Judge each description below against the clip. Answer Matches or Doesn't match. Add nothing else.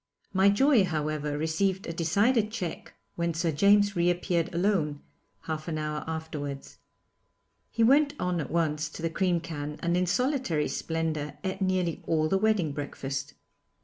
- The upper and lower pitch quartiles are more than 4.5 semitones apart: Doesn't match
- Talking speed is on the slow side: Doesn't match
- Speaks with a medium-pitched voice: Matches